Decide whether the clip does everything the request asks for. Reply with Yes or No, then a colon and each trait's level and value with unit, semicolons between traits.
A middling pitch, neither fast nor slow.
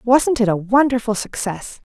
No: high, 230 Hz; average, 155 wpm